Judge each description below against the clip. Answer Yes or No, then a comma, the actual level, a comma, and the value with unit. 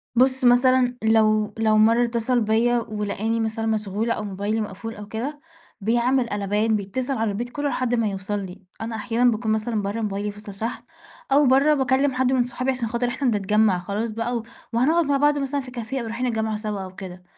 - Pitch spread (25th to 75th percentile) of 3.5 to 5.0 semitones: No, average, 2.9 semitones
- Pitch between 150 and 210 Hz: No, high, 225 Hz